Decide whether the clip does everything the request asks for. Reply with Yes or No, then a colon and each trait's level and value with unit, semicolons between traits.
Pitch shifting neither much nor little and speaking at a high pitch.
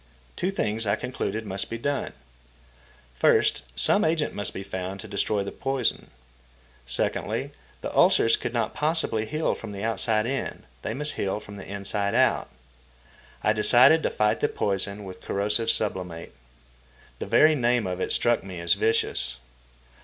No: average, 3.5 semitones; low, 105 Hz